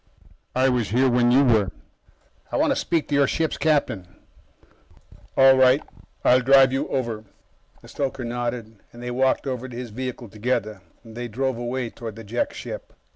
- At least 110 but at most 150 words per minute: No, average, 175 wpm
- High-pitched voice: No, low, 125 Hz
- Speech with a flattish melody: Yes, narrow, 2.2 semitones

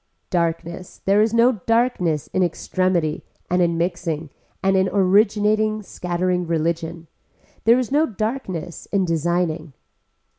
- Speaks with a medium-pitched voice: Yes, medium, 180 Hz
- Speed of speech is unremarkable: No, slow, 120 wpm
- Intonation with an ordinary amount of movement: Yes, average, 4.0 semitones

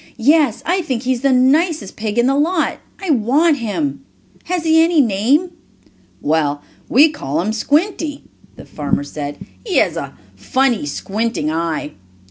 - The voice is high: Yes, very high, 260 Hz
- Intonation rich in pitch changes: Yes, wide, 7.9 semitones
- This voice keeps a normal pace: Yes, average, 155 wpm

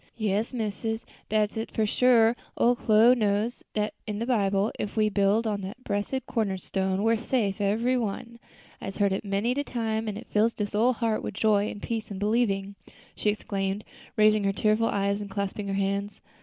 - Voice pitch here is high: Yes, high, 215 Hz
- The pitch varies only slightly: Yes, narrow, 2.1 semitones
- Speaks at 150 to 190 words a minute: No, average, 200 wpm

